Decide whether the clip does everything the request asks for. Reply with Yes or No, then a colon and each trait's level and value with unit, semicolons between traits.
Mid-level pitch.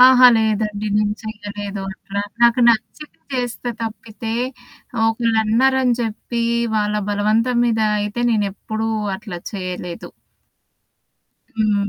No: high, 220 Hz